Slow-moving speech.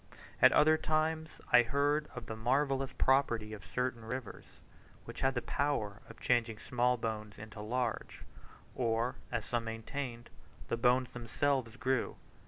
No: average, 145 wpm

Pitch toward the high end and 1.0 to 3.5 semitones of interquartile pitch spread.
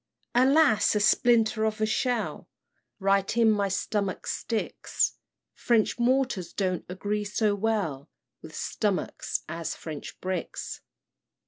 Yes: high, 210 Hz; average, 3.1 semitones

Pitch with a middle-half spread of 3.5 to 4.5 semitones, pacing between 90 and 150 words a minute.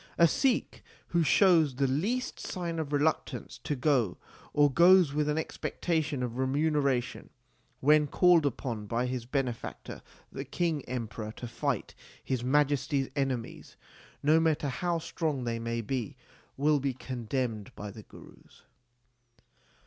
Yes: average, 4.2 semitones; average, 140 wpm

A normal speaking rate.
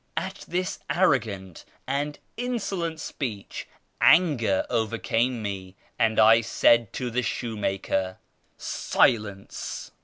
No: slow, 115 wpm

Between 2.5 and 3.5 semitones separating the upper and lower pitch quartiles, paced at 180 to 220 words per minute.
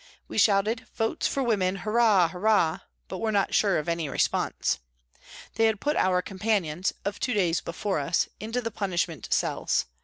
No: average, 4.2 semitones; average, 185 wpm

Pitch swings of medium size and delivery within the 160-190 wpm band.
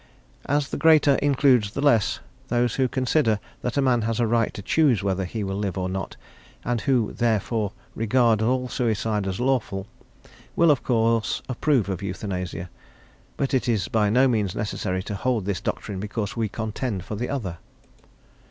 Yes: average, 4.0 semitones; average, 175 wpm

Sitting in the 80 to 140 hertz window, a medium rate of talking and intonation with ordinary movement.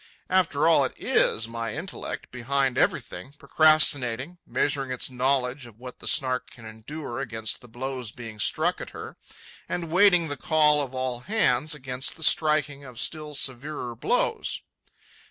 Yes: low, 135 Hz; average, 155 wpm; average, 3.7 semitones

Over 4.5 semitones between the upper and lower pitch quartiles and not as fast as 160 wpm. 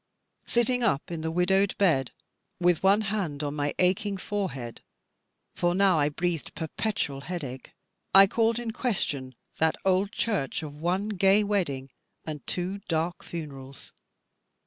Yes: average, 5.2 semitones; average, 140 wpm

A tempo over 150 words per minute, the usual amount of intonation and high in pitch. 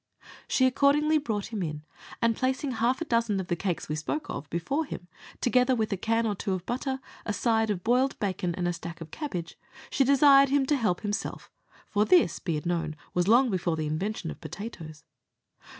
No: fast, 205 wpm; wide, 6.8 semitones; high, 215 Hz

